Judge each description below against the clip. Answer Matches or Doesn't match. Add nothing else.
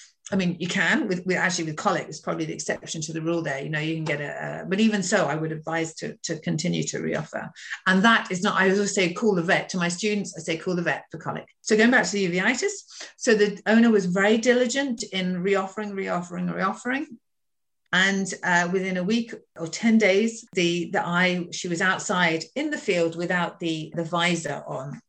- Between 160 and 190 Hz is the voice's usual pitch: Matches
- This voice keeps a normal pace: Doesn't match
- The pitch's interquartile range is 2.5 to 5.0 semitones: Matches